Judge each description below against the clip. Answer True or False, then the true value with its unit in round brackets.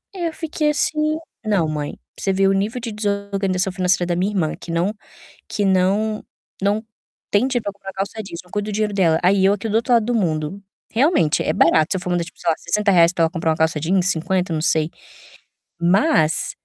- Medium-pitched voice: False (195 Hz)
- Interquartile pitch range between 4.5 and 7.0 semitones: False (3.8 semitones)